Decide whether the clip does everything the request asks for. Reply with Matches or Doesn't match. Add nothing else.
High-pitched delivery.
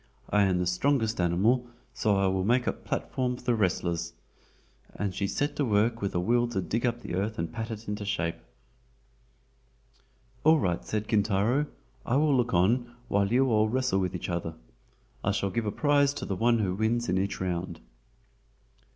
Doesn't match